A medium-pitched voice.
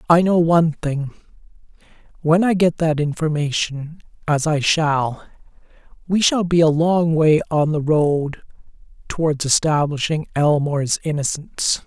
Yes: medium, 155 Hz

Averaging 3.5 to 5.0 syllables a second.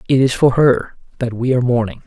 No: 6.1 syllables/s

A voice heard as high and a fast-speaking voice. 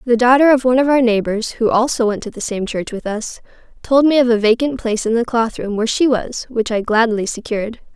Yes: high, 235 Hz; fast, 250 wpm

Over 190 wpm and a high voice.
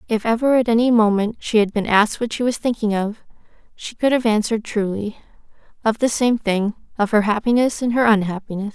Yes: average, 200 wpm; high, 220 Hz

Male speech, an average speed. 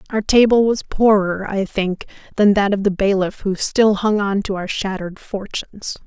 No: female; average, 190 wpm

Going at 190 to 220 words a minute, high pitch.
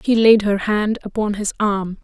Yes: fast, 205 wpm; high, 210 Hz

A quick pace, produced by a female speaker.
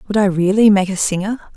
Yes: fast, 230 wpm; female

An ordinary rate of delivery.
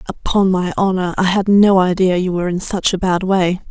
No: fast, 225 wpm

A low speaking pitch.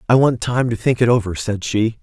Yes: low, 115 Hz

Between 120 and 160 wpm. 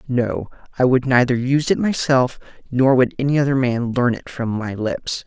No: average, 195 wpm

